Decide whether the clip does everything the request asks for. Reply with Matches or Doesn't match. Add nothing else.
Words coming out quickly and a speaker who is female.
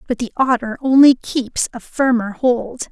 Doesn't match